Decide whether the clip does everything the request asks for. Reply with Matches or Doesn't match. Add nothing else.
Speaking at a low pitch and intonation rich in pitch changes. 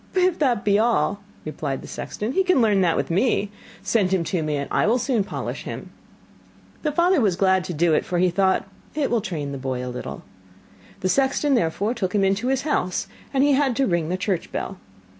Doesn't match